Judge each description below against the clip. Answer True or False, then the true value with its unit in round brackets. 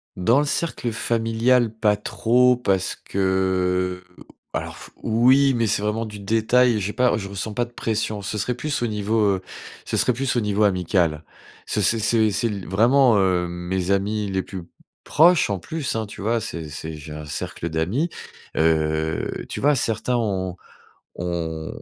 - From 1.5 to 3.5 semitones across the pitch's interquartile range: False (4.3 semitones)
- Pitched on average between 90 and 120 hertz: True (105 Hz)